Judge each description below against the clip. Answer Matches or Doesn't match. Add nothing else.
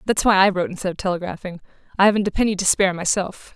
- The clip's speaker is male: Doesn't match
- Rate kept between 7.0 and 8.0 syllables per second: Matches